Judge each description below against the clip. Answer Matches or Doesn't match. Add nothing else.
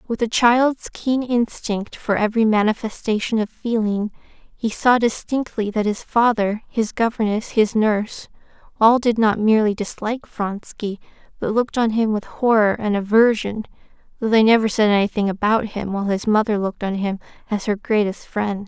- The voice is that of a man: Doesn't match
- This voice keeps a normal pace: Matches